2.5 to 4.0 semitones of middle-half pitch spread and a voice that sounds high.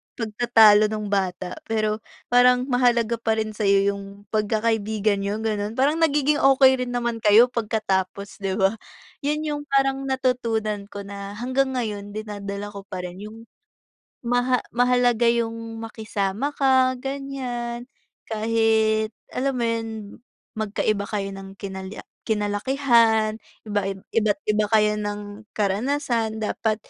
Yes: average, 3.1 semitones; high, 220 Hz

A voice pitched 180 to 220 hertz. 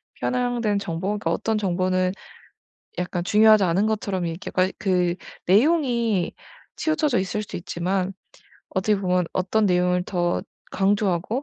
Yes: high, 190 Hz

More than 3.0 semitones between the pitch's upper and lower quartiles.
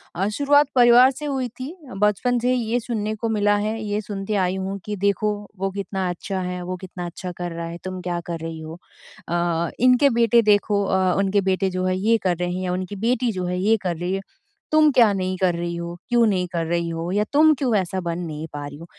Yes: average, 4.0 semitones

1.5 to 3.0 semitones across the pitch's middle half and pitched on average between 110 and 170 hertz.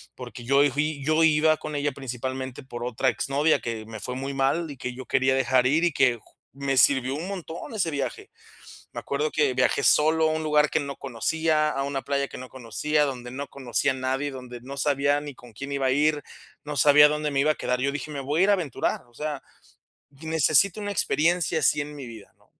Yes: average, 2.7 semitones; medium, 140 Hz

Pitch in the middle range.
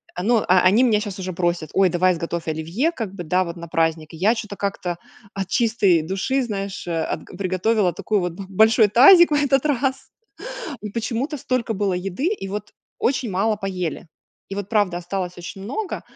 No: high, 195 Hz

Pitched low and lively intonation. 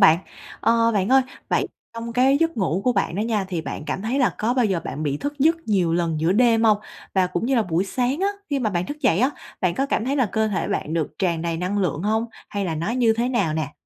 No: high, 215 Hz; wide, 6.2 semitones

